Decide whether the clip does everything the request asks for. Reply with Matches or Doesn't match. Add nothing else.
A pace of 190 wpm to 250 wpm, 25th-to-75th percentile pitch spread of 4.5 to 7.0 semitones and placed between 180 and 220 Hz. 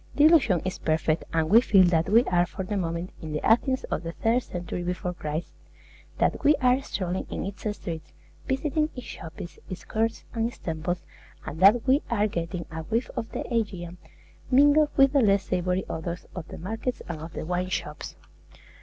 Matches